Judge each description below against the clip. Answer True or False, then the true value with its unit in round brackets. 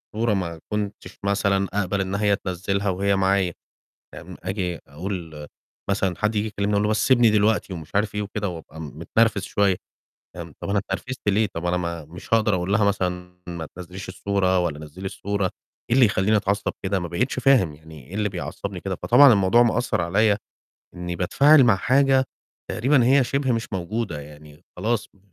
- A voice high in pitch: False (100 Hz)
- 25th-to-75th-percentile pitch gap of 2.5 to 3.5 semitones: True (3.2 semitones)